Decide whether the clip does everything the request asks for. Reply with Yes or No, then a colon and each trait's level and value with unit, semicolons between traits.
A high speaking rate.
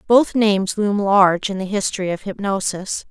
No: average, 175 wpm